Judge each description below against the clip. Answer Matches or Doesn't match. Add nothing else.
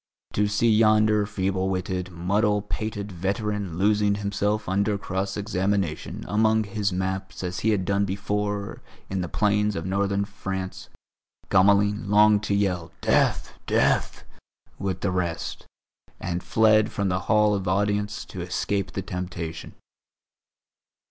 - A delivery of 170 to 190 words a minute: Doesn't match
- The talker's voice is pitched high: Doesn't match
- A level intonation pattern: Matches